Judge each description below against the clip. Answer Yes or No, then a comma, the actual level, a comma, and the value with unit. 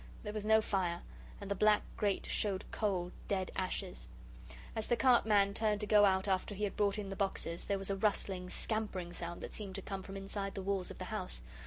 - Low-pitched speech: No, high, 195 Hz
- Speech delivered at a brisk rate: Yes, fast, 225 wpm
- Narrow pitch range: Yes, narrow, 1.8 semitones